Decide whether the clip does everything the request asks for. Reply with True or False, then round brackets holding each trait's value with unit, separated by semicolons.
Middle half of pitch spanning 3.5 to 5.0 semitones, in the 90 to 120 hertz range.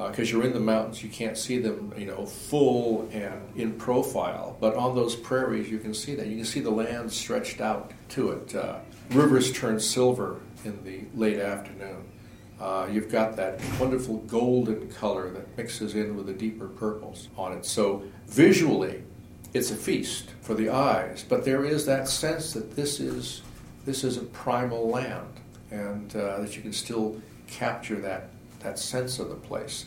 False (2.9 semitones; 110 Hz)